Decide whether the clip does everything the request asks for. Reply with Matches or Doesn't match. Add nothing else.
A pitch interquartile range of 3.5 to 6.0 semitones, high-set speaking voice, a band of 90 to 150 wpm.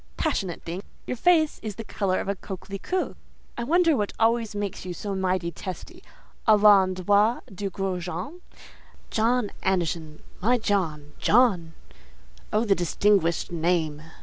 Matches